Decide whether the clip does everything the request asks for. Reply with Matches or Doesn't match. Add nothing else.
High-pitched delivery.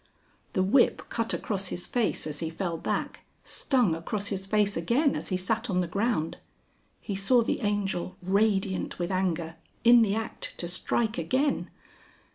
Matches